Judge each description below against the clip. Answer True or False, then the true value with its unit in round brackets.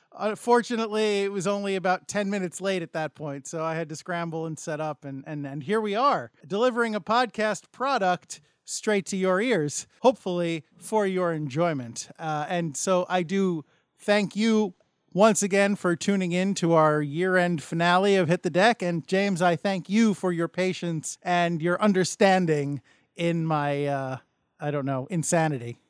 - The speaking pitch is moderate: True (180 Hz)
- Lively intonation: False (4.1 semitones)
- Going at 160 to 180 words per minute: True (175 wpm)